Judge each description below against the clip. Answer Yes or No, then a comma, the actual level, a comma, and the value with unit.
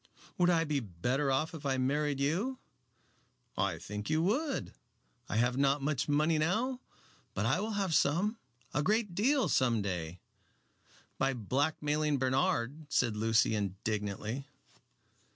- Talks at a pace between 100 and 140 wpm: Yes, slow, 135 wpm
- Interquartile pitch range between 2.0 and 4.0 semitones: No, wide, 5.6 semitones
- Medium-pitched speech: Yes, medium, 145 Hz